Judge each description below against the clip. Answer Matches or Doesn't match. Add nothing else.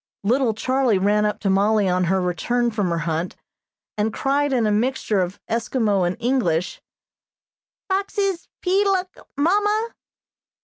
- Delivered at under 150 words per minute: Matches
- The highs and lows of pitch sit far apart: Matches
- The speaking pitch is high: Matches